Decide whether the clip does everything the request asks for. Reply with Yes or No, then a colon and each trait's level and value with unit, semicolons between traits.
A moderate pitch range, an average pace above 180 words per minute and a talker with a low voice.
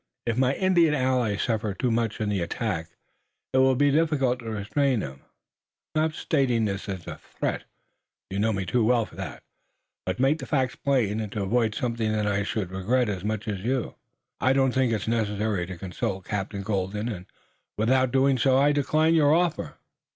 Yes: average, 4.5 semitones; average, 195 wpm; low, 115 Hz